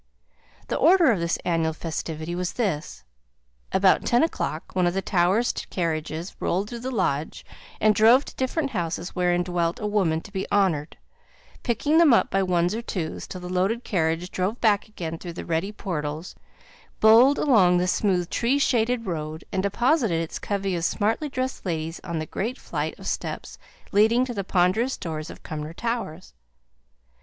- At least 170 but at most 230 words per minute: Yes, average, 175 wpm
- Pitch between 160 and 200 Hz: Yes, medium, 185 Hz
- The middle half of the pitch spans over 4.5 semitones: Yes, average, 5.3 semitones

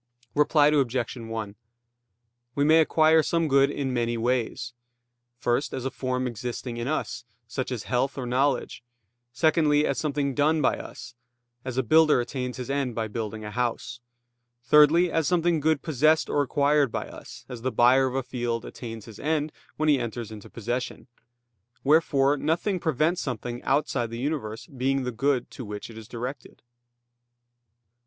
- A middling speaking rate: Yes, average, 165 wpm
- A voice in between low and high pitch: No, low, 130 Hz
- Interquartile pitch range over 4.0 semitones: No, average, 3.7 semitones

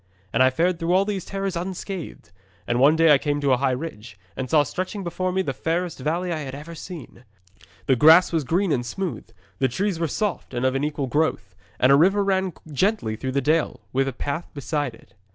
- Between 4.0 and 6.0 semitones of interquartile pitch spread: Yes, average, 5.2 semitones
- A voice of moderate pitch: Yes, medium, 155 Hz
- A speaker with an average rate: No, fast, 225 wpm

